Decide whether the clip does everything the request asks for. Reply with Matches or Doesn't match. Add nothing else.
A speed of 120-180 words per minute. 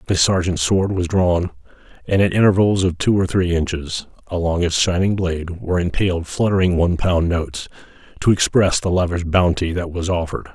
Matches